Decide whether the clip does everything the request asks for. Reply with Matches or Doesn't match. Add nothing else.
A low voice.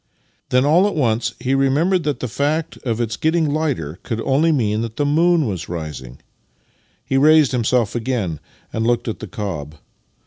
Matches